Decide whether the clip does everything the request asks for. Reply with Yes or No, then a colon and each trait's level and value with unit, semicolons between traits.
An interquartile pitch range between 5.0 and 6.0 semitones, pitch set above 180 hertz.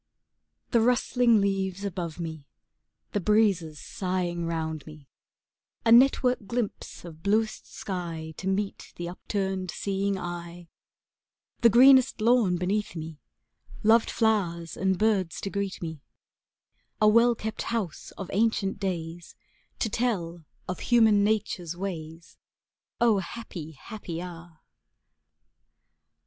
No: average, 4.3 semitones; high, 190 Hz